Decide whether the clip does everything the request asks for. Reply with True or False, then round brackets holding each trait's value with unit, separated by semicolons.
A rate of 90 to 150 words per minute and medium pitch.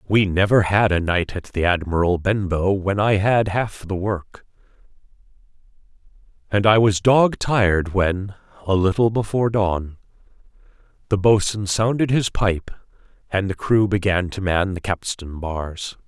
False (145 wpm; 100 Hz)